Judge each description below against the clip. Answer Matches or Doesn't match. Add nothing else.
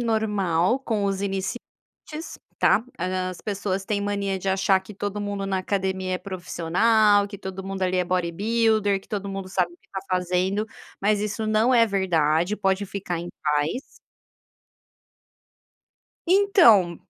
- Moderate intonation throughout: Doesn't match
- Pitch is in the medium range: Doesn't match